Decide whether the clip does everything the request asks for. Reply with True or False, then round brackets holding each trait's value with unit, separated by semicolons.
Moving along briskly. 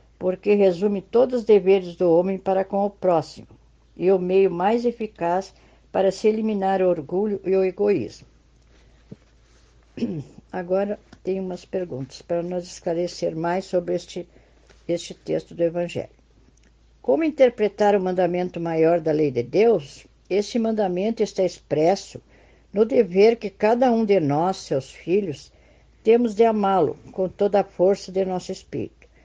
False (145 wpm)